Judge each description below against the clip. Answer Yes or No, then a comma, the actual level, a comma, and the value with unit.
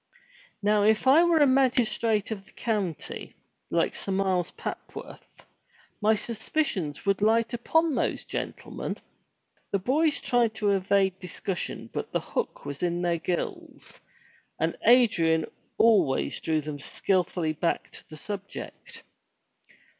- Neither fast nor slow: No, slow, 130 wpm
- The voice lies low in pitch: No, high, 205 Hz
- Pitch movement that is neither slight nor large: Yes, average, 4.7 semitones